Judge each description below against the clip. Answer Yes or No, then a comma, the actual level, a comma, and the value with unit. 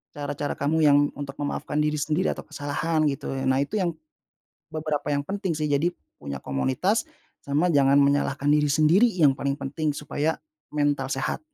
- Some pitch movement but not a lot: No, narrow, 2.0 semitones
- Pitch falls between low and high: Yes, medium, 145 Hz